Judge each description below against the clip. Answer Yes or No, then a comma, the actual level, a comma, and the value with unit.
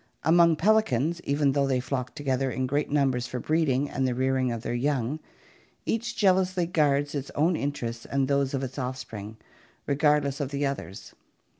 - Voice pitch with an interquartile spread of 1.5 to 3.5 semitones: Yes, average, 2.7 semitones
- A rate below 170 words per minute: No, average, 175 wpm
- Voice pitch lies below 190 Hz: Yes, medium, 140 Hz